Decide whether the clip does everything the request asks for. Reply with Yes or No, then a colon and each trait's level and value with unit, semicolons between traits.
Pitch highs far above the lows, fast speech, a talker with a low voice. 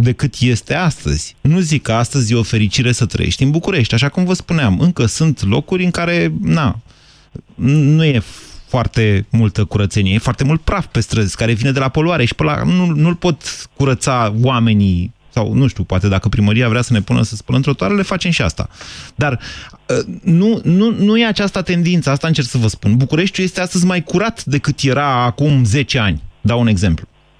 Yes: wide, 6.7 semitones; fast, 195 wpm; low, 130 Hz